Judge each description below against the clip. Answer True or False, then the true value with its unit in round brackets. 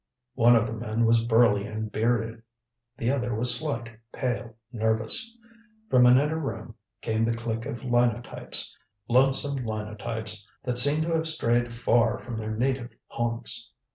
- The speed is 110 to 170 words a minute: True (150 wpm)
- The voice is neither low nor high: False (115 Hz)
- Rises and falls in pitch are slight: True (1.8 semitones)